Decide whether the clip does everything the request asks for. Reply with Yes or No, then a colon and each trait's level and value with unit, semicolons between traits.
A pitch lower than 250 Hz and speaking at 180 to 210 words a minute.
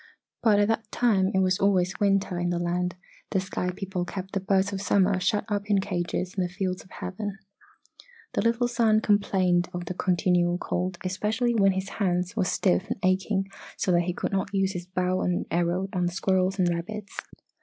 Yes: high, 190 Hz; average, 200 wpm